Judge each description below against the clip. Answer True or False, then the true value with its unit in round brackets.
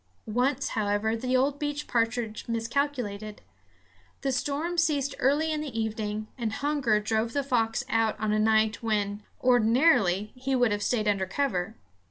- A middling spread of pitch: True (4.2 semitones)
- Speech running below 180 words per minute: True (155 wpm)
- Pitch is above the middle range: True (230 Hz)